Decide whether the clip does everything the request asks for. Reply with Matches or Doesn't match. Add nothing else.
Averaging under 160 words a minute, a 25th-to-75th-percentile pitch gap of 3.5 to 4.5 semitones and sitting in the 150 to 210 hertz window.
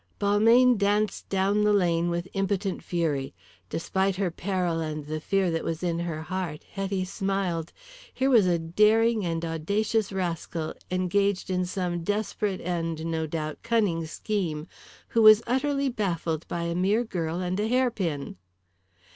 Matches